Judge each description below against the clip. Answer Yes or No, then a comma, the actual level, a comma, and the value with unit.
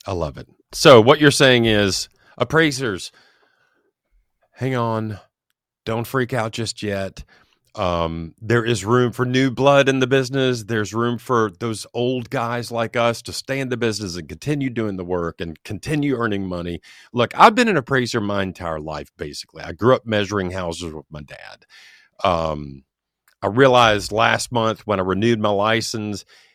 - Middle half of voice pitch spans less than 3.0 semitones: No, average, 5.0 semitones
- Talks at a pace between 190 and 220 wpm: No, average, 170 wpm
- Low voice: Yes, low, 115 Hz